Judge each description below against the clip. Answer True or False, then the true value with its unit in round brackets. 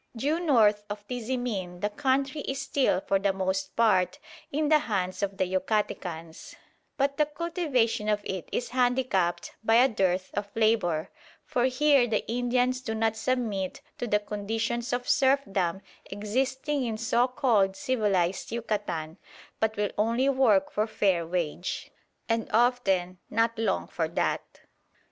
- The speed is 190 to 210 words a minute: False (145 wpm)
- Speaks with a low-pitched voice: False (220 Hz)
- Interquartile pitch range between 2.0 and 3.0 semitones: False (4.7 semitones)